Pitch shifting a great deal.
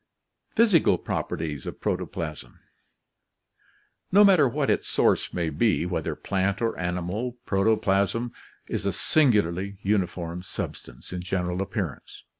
No: average, 4.6 semitones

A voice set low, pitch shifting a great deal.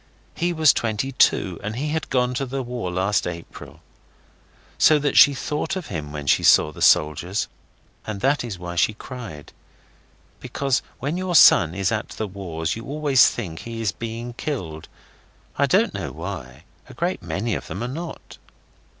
Yes: low, 115 Hz; wide, 7.4 semitones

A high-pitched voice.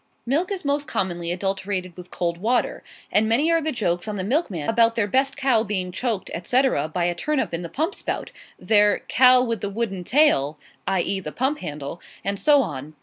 Yes: high, 205 Hz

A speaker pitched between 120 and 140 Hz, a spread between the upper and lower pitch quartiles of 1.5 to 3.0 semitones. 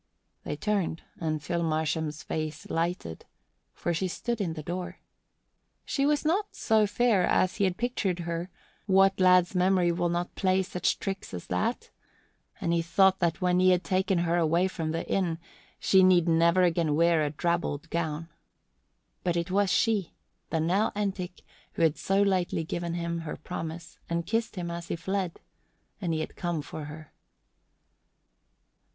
No: medium, 175 Hz; narrow, 2.4 semitones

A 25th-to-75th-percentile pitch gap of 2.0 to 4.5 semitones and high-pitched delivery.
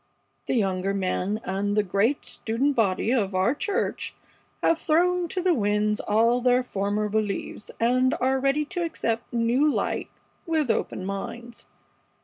No: average, 5.1 semitones; high, 230 Hz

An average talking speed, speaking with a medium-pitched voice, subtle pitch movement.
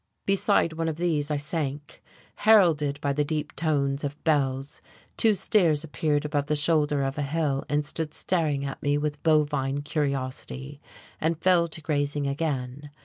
Yes: average, 160 wpm; medium, 150 Hz; narrow, 2.1 semitones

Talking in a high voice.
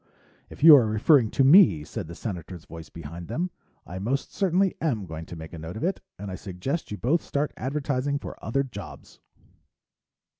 No: low, 115 Hz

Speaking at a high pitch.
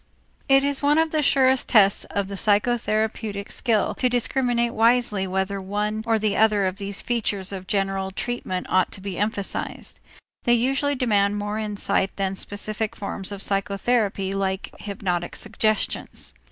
Yes: high, 210 Hz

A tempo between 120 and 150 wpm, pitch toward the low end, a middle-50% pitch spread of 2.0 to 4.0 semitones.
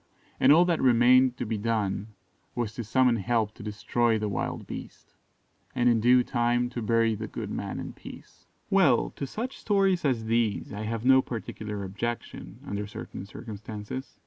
No: average, 170 wpm; low, 115 Hz; average, 2.8 semitones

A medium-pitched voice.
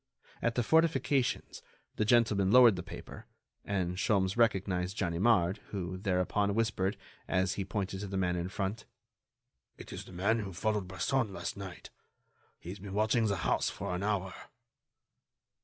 No: low, 100 Hz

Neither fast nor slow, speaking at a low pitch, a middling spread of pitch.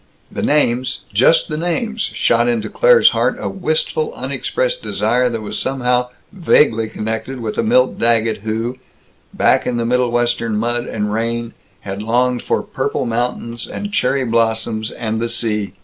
No: average, 155 wpm; low, 120 Hz; narrow, 2.2 semitones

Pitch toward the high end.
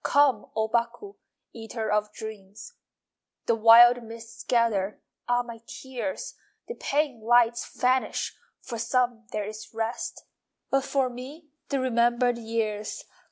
Yes: high, 235 Hz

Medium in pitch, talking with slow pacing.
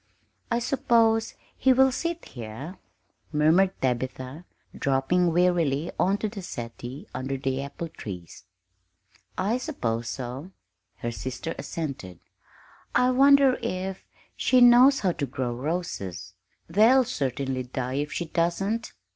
Yes: medium, 165 Hz; slow, 120 wpm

